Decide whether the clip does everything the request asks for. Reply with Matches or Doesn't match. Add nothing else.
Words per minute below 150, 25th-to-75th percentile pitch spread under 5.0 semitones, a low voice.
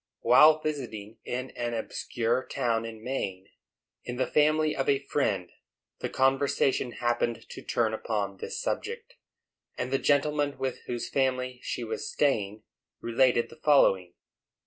Matches